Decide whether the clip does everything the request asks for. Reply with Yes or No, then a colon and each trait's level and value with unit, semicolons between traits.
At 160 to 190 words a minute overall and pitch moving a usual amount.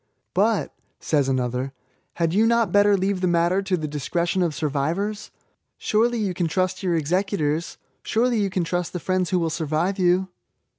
Yes: average, 170 wpm; average, 3.6 semitones